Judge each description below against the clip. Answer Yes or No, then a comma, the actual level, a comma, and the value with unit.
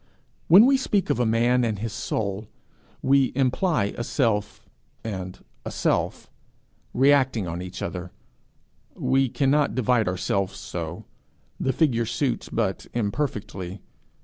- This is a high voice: No, low, 115 Hz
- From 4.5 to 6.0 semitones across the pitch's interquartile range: Yes, average, 5.1 semitones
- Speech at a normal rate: No, slow, 125 wpm